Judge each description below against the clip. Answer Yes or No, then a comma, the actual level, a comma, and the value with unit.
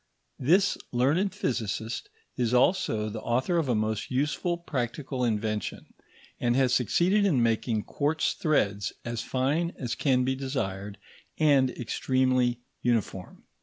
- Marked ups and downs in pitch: No, average, 4.3 semitones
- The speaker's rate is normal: No, slow, 130 wpm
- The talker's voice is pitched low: Yes, low, 125 Hz